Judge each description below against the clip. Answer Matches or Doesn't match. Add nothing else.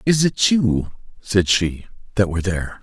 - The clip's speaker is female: Doesn't match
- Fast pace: Doesn't match